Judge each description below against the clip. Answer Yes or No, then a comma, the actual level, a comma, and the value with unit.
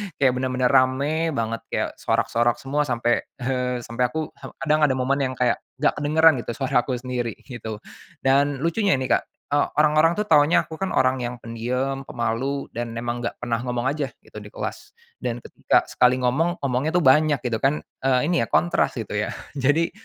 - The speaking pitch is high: No, low, 130 Hz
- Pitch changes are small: No, average, 3.3 semitones